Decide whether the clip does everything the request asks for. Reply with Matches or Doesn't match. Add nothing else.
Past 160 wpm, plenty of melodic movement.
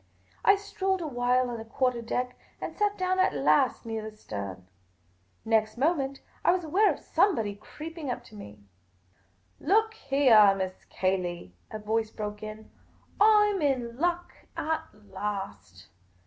Doesn't match